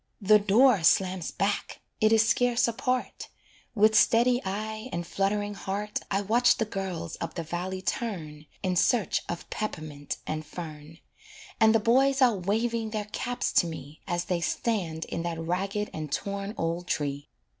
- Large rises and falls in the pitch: No, average, 4.7 semitones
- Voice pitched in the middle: No, high, 195 Hz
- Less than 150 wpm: No, average, 160 wpm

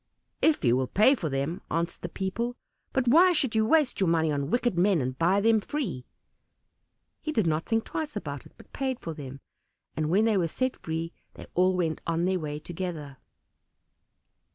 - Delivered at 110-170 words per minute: No, average, 195 wpm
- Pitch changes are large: Yes, wide, 6.7 semitones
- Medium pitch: Yes, medium, 180 Hz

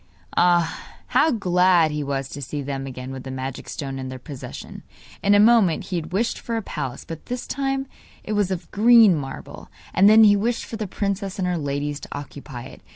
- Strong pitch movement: Yes, wide, 6.8 semitones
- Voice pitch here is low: No, medium, 175 Hz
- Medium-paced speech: No, fast, 215 wpm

